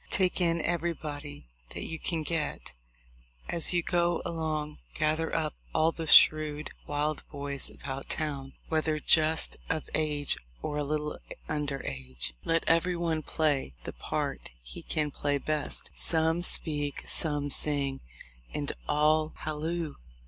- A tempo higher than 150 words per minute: No, average, 140 wpm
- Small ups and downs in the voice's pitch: Yes, narrow, 1.9 semitones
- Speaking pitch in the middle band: Yes, medium, 155 Hz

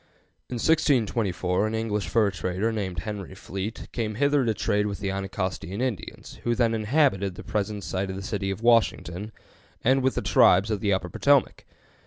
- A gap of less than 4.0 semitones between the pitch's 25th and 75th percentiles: Yes, average, 3.2 semitones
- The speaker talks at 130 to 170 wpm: No, average, 180 wpm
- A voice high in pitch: No, low, 105 Hz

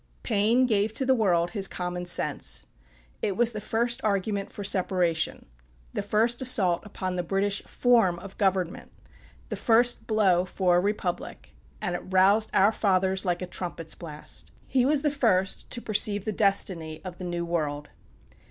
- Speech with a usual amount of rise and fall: Yes, average, 3.5 semitones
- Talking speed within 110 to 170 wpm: Yes, average, 165 wpm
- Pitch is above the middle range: Yes, high, 195 Hz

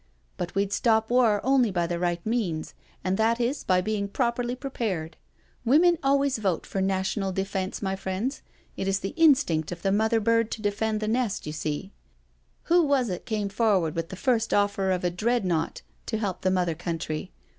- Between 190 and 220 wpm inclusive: Yes, average, 195 wpm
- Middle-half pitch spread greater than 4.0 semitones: Yes, average, 4.4 semitones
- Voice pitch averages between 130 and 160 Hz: No, high, 200 Hz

